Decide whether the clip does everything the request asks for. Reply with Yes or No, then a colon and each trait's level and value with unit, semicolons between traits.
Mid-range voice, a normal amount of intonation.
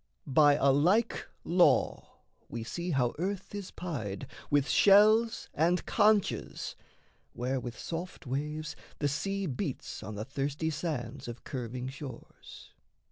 No: medium, 150 Hz; wide, 5.7 semitones